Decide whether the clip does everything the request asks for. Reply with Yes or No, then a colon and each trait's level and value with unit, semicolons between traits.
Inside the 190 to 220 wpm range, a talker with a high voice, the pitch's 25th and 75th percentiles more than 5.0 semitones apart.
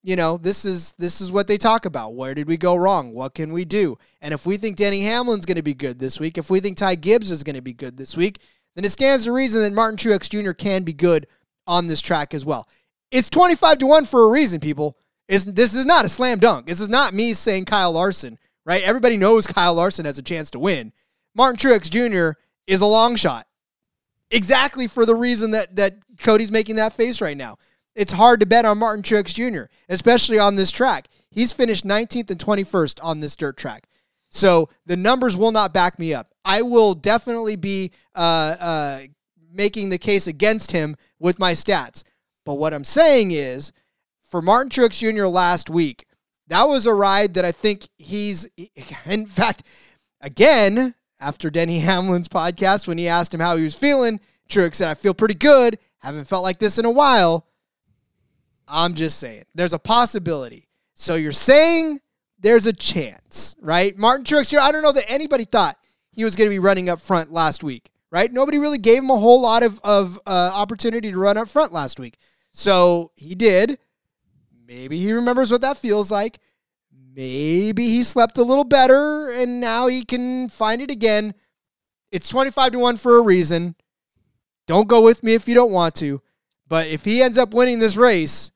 Yes: average, 200 wpm; high, 200 Hz; wide, 5.5 semitones